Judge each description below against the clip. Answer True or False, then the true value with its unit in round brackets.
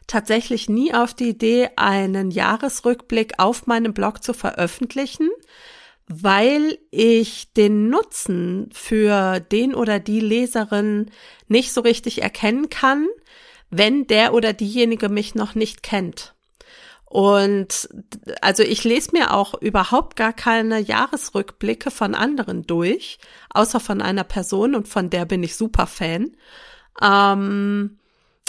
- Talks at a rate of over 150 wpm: False (125 wpm)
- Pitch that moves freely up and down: False (3.3 semitones)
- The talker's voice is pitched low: False (220 Hz)